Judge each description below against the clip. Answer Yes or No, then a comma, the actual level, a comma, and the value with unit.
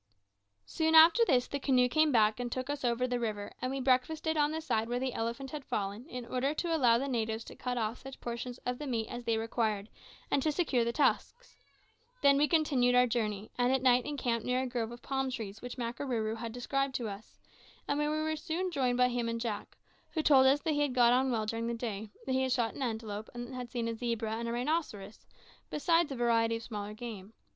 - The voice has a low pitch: No, high, 245 Hz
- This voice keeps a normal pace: No, fast, 235 wpm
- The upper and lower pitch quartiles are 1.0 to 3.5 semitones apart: Yes, average, 3.1 semitones